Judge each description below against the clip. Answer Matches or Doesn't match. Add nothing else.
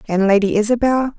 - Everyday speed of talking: Matches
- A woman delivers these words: Matches